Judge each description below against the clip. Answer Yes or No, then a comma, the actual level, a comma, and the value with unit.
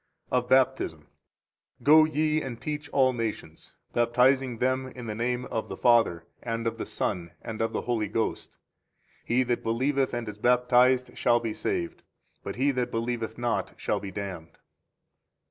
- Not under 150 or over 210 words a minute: Yes, average, 165 wpm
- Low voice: Yes, low, 120 Hz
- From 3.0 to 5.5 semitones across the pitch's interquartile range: No, narrow, 2.4 semitones